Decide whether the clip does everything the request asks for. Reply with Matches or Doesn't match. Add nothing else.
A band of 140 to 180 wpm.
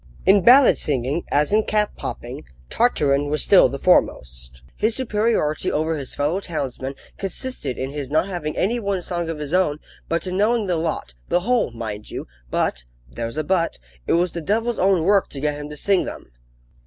Doesn't match